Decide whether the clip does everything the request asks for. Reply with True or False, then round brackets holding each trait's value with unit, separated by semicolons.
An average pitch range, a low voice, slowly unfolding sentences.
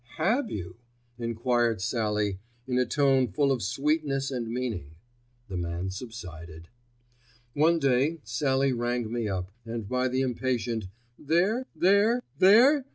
True (4.9 semitones; 125 Hz; 130 wpm)